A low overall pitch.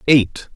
Yes: low, 125 Hz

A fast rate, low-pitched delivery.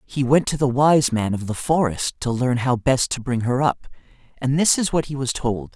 Yes: fast, 250 wpm; low, 130 Hz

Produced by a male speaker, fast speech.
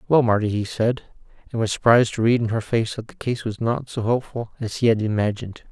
Yes: male; fast, 240 wpm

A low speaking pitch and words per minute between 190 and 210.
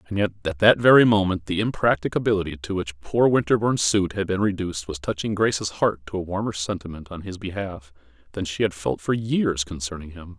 Yes: very low, 95 Hz; average, 200 wpm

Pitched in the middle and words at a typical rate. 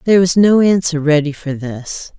Yes: medium, 165 Hz; average, 190 wpm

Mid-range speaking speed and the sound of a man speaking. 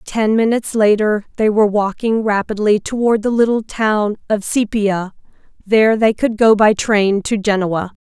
No: average, 155 wpm; female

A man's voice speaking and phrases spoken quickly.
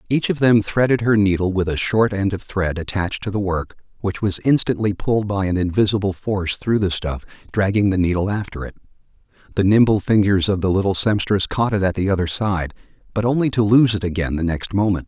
Yes: male; fast, 215 wpm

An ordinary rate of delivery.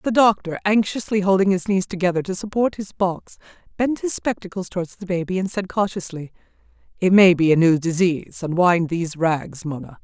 Yes: average, 180 wpm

